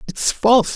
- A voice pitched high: Yes, high, 225 Hz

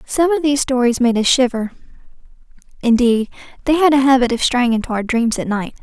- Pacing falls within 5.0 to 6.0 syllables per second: No, 2.9 syllables/s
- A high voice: Yes, very high, 250 Hz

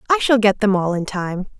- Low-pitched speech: No, high, 205 Hz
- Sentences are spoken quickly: Yes, fast, 265 wpm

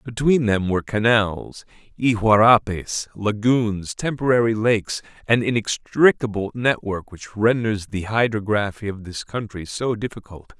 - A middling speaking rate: No, slow, 115 wpm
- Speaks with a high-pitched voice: No, low, 110 Hz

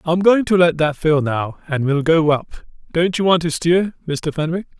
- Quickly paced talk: Yes, fast, 225 wpm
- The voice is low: No, medium, 165 Hz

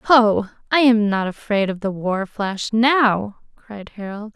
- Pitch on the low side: No, high, 215 Hz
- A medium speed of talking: Yes, average, 165 wpm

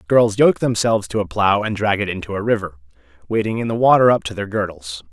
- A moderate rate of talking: No, fast, 235 wpm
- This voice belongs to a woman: No, male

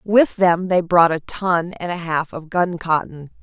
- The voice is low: No, medium, 175 Hz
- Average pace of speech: Yes, average, 190 wpm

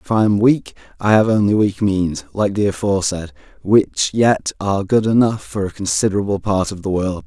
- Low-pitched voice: Yes, low, 100 Hz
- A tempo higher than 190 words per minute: Yes, average, 200 wpm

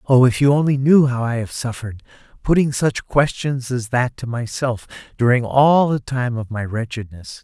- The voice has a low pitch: Yes, low, 125 Hz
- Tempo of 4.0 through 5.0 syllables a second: Yes, 4.8 syllables/s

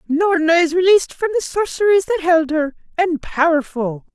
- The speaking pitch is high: Yes, very high, 325 Hz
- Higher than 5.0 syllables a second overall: Yes, 5.3 syllables/s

